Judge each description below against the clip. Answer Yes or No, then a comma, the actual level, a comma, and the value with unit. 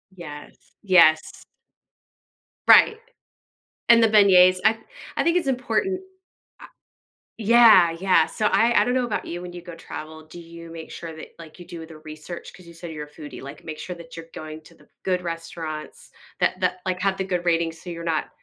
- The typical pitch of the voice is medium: Yes, medium, 170 Hz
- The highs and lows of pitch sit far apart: No, average, 3.1 semitones